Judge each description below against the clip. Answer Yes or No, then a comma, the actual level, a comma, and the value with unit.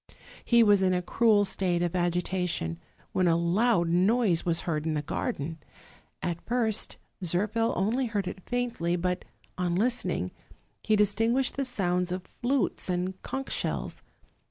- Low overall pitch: No, medium, 185 Hz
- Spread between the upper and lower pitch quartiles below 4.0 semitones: No, average, 4.5 semitones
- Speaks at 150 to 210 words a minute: Yes, average, 155 wpm